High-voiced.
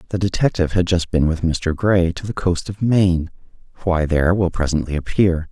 No: very low, 90 Hz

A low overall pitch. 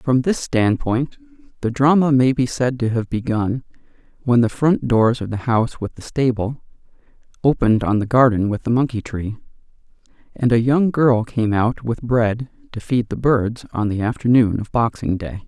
Yes: low, 120 Hz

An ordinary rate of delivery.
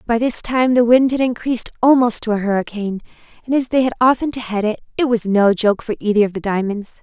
No: fast, 240 wpm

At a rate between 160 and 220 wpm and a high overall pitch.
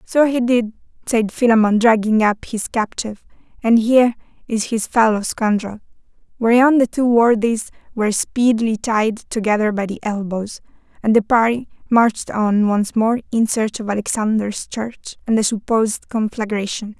No: average, 150 wpm; high, 220 Hz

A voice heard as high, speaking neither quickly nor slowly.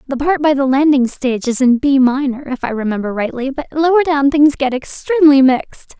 No: very high, 275 Hz; fast, 210 wpm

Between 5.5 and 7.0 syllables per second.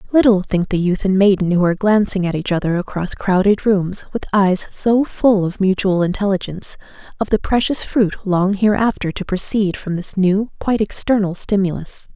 No: 5.1 syllables/s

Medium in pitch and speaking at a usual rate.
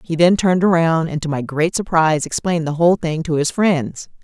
No: medium, 165 Hz; fast, 225 wpm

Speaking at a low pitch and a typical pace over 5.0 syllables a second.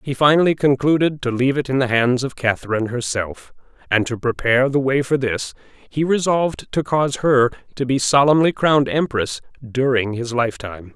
Yes: low, 130 Hz; 5.6 syllables/s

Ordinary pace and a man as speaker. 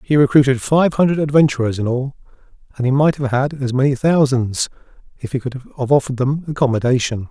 Yes: average, 180 wpm; male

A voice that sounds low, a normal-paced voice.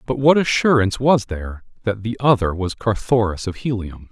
Yes: low, 110 Hz; average, 175 wpm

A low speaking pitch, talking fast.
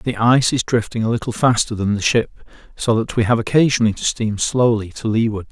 Yes: low, 115 Hz; fast, 220 wpm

